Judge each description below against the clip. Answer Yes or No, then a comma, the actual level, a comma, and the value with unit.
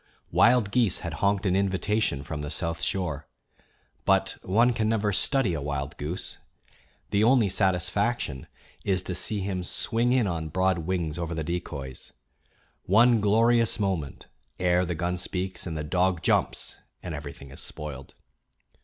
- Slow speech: No, average, 155 wpm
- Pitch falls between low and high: No, very low, 90 Hz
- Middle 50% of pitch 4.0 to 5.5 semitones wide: Yes, average, 4.5 semitones